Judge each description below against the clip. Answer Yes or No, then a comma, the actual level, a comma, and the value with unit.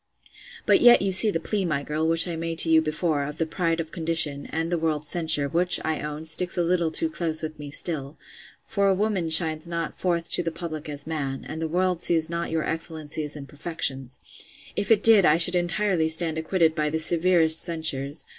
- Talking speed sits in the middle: No, fast, 215 wpm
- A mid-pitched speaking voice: Yes, medium, 165 Hz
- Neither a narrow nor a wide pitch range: No, narrow, 2.0 semitones